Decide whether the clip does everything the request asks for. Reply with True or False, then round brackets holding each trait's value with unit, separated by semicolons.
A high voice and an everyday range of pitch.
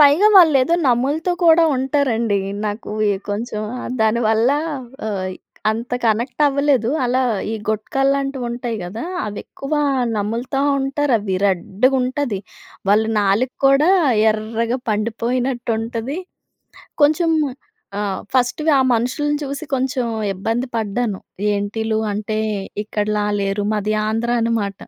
True (235 Hz; 4.1 semitones)